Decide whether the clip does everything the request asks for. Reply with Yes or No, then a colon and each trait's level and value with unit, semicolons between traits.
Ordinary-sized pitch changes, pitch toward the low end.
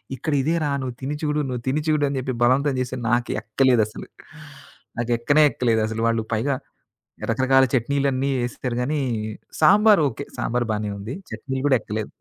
Yes: average, 3.4 semitones; low, 130 Hz